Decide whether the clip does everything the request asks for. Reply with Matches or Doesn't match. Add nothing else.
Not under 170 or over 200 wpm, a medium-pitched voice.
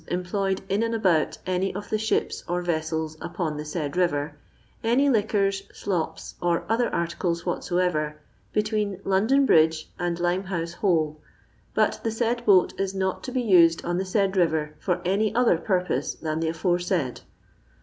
Doesn't match